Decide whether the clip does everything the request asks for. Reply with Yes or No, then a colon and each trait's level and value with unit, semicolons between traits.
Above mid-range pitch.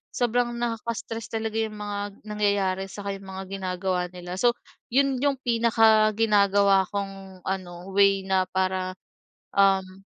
Yes: high, 200 Hz